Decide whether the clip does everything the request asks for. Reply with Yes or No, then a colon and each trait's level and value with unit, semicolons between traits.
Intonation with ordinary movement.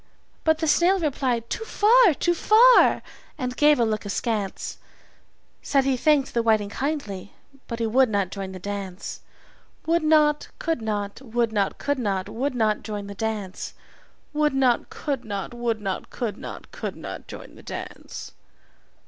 No: wide, 6.3 semitones